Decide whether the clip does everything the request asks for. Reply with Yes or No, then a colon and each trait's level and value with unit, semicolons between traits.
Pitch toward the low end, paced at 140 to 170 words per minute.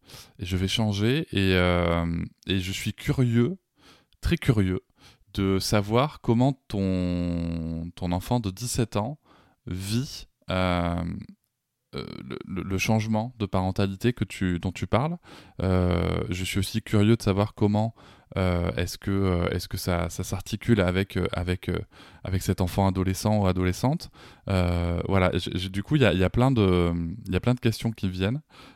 Yes: very low, 95 Hz; average, 150 wpm